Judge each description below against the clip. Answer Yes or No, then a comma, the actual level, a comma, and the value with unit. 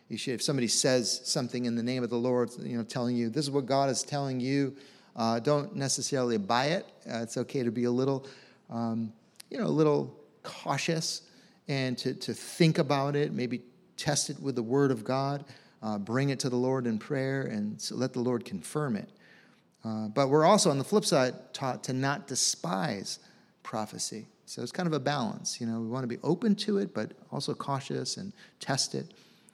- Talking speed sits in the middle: No, fast, 210 wpm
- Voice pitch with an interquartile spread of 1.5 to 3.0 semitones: No, average, 3.6 semitones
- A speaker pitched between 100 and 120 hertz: No, low, 135 Hz